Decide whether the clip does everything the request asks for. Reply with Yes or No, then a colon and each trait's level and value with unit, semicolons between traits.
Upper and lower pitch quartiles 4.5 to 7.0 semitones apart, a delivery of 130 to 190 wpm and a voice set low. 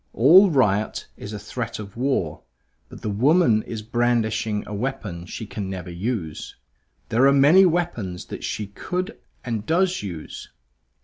Yes: wide, 5.4 semitones; average, 150 wpm; low, 115 Hz